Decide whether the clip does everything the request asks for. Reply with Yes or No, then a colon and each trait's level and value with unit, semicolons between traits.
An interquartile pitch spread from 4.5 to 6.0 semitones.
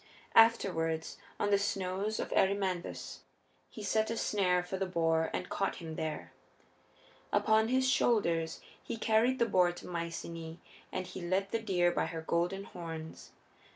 No: average, 3.9 semitones